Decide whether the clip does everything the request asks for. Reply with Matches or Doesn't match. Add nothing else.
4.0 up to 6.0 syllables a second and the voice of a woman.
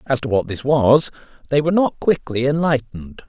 Doesn't match